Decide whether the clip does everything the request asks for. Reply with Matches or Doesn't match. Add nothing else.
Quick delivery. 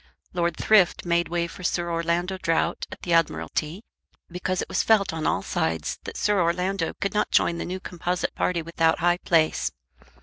Doesn't match